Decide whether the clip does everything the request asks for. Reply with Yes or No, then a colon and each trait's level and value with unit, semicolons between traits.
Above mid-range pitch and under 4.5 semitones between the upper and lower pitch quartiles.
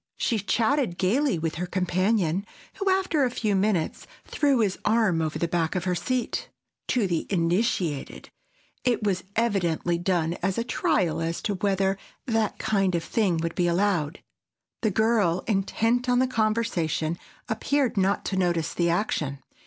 No: high, 195 Hz; average, 4.8 semitones